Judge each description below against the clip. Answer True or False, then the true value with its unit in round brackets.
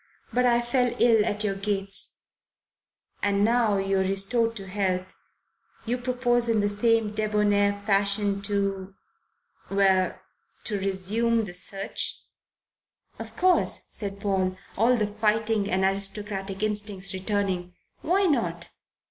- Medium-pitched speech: False (205 Hz)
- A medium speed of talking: False (125 wpm)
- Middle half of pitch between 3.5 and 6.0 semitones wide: False (2.5 semitones)